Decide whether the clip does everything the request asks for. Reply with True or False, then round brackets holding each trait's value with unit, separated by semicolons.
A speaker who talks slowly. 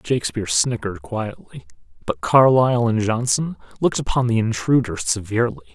True (125 wpm)